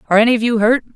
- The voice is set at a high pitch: Yes, high, 230 Hz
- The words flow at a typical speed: No, fast, 315 wpm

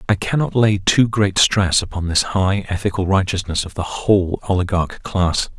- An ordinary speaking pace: Yes, average, 170 wpm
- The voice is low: Yes, very low, 95 Hz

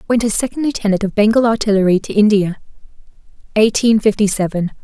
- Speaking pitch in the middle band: No, high, 210 Hz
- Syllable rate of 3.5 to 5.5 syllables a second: No, 6.4 syllables/s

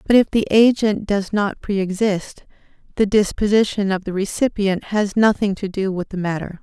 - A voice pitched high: Yes, high, 200 Hz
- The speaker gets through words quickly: No, average, 180 wpm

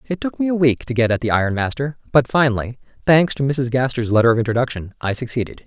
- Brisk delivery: Yes, fast, 235 wpm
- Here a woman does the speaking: No, male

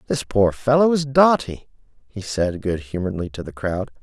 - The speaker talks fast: No, average, 180 wpm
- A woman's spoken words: No, male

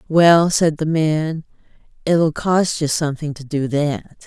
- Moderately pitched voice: Yes, medium, 155 Hz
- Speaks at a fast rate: No, average, 155 wpm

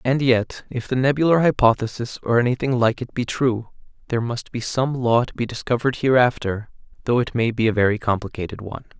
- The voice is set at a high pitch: No, low, 120 Hz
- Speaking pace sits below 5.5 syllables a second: No, 5.9 syllables/s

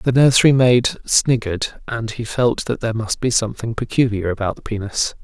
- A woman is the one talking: No, male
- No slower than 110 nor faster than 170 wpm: No, average, 185 wpm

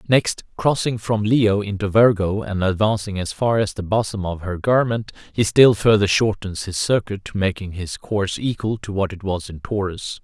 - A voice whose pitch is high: No, low, 100 Hz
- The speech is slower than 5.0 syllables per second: Yes, 4.7 syllables/s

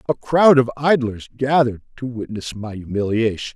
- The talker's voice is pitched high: No, low, 120 Hz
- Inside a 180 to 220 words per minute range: No, average, 150 wpm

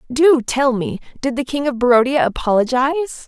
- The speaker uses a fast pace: No, average, 165 wpm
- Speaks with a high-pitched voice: Yes, very high, 260 Hz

